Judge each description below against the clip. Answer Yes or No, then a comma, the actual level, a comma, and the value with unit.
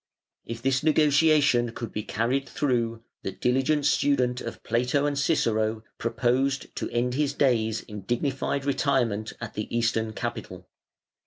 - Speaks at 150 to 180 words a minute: No, average, 140 wpm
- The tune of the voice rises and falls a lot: No, average, 3.5 semitones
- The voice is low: Yes, low, 125 Hz